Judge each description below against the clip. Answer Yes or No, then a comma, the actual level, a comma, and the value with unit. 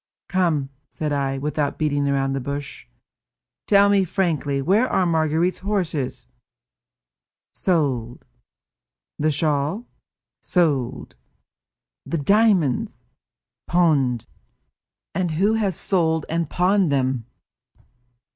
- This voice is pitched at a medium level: Yes, medium, 155 Hz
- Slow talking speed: Yes, slow, 95 wpm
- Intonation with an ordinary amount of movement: Yes, average, 4.9 semitones